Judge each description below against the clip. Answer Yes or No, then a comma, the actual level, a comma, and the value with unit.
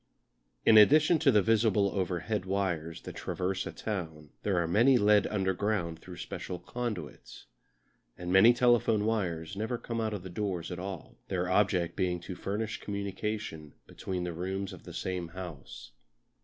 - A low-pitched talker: Yes, very low, 95 Hz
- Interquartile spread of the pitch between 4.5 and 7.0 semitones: No, average, 3.3 semitones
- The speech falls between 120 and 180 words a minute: Yes, average, 155 wpm